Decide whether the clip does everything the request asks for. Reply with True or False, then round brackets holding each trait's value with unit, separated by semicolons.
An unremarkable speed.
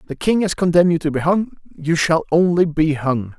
False (230 wpm)